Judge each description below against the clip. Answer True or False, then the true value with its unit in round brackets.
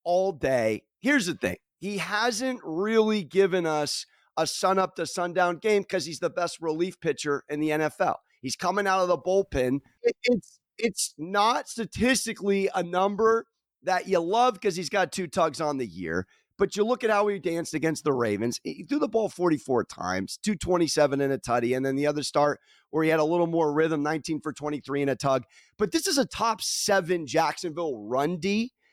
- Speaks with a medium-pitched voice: True (175 Hz)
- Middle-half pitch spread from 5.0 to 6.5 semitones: True (5.4 semitones)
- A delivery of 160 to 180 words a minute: False (195 wpm)